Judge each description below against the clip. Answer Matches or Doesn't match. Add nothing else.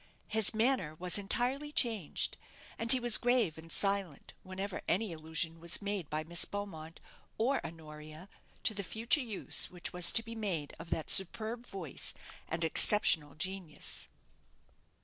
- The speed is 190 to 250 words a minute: Doesn't match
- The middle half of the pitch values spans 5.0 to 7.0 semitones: Matches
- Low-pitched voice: Doesn't match